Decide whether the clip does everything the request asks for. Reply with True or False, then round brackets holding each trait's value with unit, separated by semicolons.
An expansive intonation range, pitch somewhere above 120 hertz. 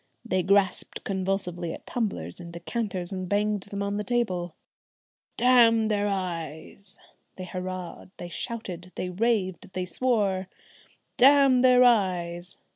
False (3.6 semitones; 190 Hz)